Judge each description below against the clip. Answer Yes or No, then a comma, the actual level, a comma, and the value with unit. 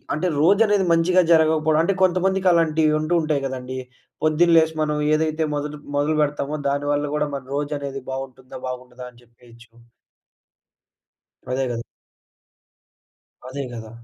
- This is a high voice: No, medium, 150 Hz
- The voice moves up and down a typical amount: Yes, average, 3.2 semitones